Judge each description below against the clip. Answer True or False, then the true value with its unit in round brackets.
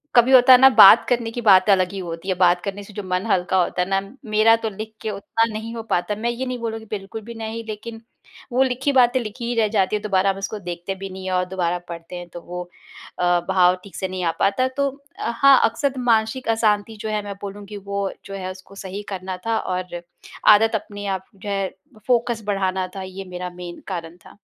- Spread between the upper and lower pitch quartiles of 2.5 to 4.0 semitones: True (3.4 semitones)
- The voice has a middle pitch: False (200 Hz)